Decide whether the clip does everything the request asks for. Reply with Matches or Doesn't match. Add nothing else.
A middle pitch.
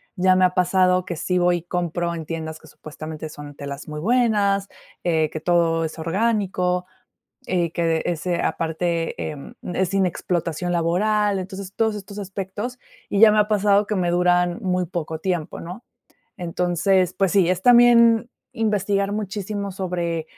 Matches